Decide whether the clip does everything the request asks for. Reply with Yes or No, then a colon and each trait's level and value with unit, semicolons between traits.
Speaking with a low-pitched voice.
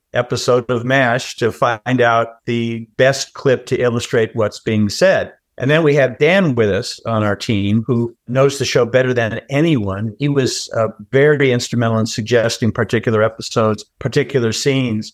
Yes: low, 120 Hz